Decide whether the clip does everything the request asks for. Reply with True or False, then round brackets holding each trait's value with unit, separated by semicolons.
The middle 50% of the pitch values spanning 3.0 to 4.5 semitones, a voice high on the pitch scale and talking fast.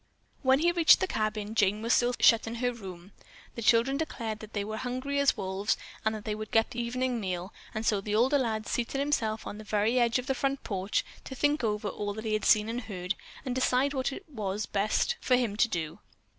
True (3.3 semitones; 225 Hz; 235 wpm)